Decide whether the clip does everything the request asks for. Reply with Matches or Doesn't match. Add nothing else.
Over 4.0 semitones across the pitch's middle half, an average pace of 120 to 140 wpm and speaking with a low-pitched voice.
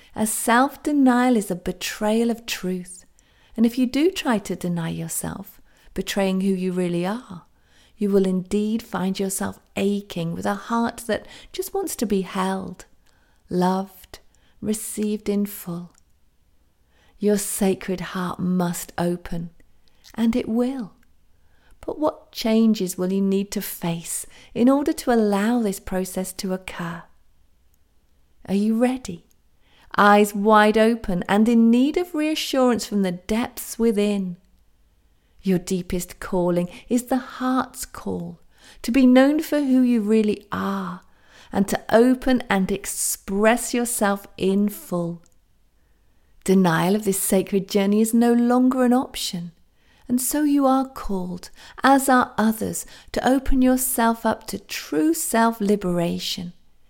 Doesn't match